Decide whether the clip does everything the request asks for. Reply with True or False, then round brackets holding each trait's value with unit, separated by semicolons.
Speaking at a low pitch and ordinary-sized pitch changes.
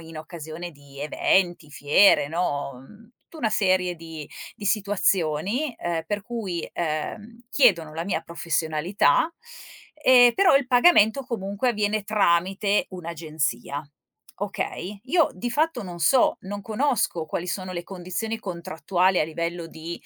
False (185 Hz; 4.8 semitones)